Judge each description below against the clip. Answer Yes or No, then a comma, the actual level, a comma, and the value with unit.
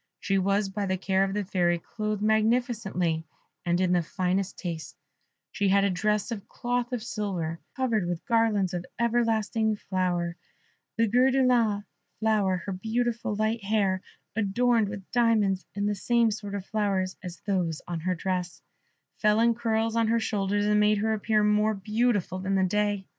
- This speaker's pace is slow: No, average, 175 wpm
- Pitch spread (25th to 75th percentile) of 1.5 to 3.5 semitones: Yes, average, 2.9 semitones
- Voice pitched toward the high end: Yes, high, 205 Hz